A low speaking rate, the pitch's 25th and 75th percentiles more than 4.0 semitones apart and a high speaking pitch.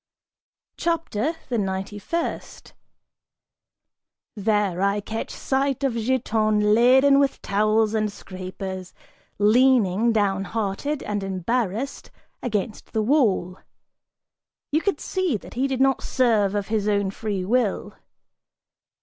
Yes: slow, 110 wpm; average, 4.5 semitones; high, 215 Hz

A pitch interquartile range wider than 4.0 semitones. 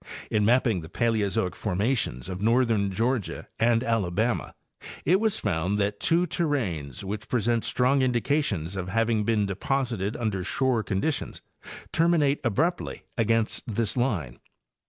Yes: average, 4.5 semitones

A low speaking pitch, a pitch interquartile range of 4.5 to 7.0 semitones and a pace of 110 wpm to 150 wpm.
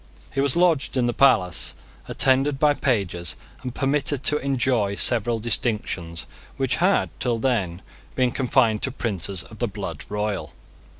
Yes: low, 120 Hz; average, 5.1 semitones; average, 145 wpm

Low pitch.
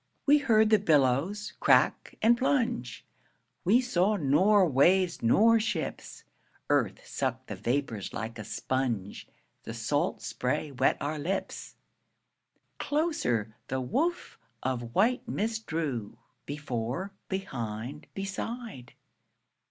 No: medium, 165 Hz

